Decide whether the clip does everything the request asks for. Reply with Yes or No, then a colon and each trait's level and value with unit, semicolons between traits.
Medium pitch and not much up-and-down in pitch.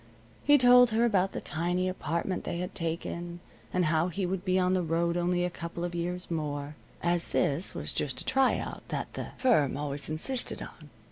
Yes: medium, 175 Hz; narrow, 2.1 semitones